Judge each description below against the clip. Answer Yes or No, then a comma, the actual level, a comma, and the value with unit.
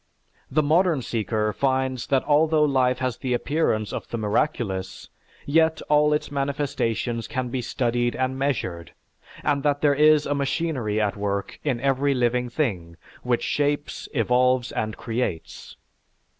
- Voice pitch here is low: Yes, low, 130 Hz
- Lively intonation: No, average, 3.8 semitones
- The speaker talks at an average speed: Yes, average, 145 wpm